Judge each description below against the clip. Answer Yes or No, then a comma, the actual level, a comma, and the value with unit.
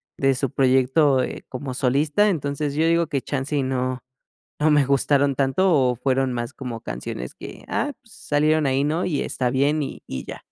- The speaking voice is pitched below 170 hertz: Yes, medium, 140 Hz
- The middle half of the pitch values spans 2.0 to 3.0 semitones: Yes, narrow, 2.5 semitones